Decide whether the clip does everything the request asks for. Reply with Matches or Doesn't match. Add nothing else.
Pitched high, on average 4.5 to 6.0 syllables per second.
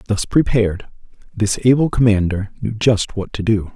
Doesn't match